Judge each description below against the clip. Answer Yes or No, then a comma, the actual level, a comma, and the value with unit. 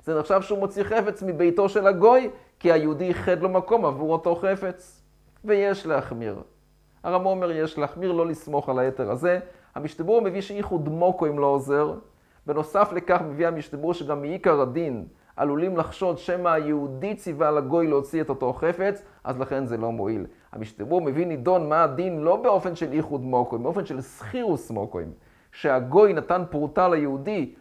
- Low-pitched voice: No, medium, 165 Hz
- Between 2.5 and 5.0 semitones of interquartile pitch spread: Yes, average, 4.0 semitones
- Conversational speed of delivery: No, fast, 160 wpm